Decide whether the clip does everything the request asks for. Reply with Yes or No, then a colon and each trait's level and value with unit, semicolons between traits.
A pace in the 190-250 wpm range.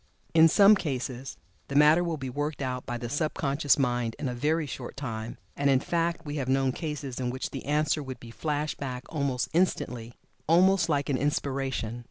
Yes: average, 200 wpm